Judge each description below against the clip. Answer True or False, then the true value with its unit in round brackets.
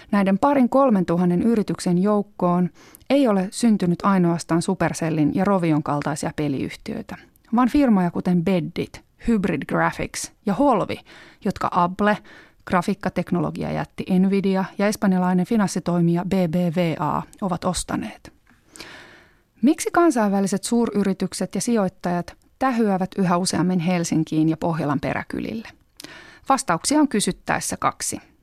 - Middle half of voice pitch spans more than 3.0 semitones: True (3.4 semitones)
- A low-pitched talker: False (185 Hz)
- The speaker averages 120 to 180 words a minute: False (105 wpm)